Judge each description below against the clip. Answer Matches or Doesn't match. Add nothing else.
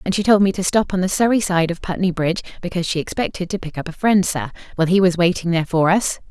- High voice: Doesn't match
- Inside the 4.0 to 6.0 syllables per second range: Doesn't match